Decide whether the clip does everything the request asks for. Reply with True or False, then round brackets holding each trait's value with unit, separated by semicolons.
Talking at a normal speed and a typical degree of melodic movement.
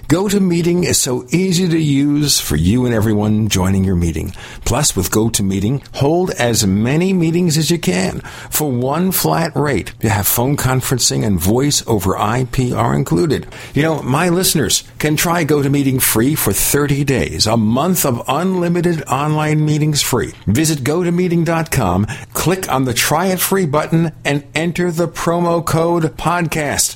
False (155 wpm; 6.2 semitones)